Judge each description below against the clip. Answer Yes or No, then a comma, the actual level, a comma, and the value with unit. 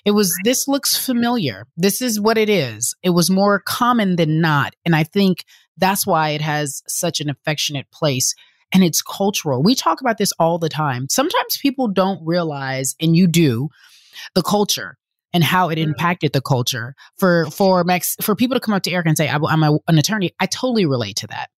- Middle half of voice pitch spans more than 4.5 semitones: Yes, average, 5.0 semitones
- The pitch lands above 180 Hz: No, medium, 175 Hz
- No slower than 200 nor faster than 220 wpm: Yes, fast, 205 wpm